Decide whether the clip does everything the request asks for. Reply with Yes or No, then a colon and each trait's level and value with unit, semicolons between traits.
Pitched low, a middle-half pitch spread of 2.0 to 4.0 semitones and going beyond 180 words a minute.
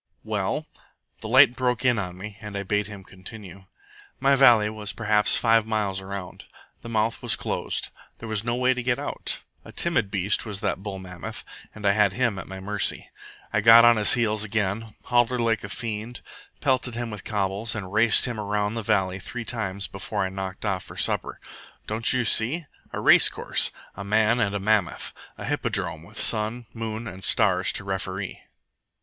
Yes: low, 105 Hz; average, 2.8 semitones; average, 190 wpm